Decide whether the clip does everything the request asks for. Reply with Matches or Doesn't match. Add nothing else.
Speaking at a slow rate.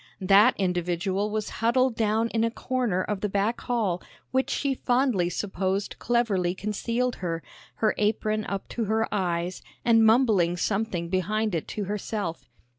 Doesn't match